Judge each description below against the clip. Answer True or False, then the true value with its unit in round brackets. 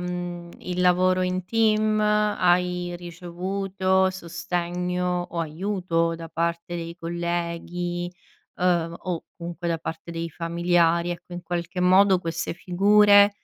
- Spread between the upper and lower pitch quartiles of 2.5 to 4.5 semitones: False (1.4 semitones)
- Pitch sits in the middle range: True (175 Hz)